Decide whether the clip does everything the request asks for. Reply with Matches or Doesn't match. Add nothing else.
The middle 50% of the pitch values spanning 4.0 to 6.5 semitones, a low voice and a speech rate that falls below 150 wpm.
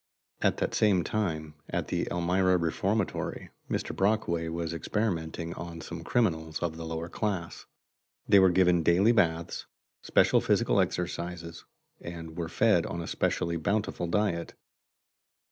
Doesn't match